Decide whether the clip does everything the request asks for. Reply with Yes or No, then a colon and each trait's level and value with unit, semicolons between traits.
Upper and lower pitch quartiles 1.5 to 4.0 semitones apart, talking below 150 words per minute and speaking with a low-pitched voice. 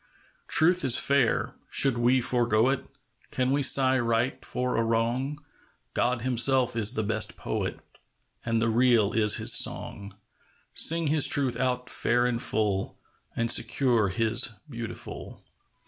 Yes: narrow, 2.5 semitones; average, 140 wpm; low, 120 Hz